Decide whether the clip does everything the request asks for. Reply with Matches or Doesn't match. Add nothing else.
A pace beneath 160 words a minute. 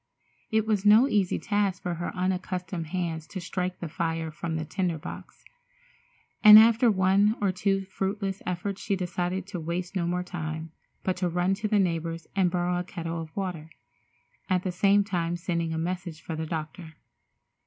Doesn't match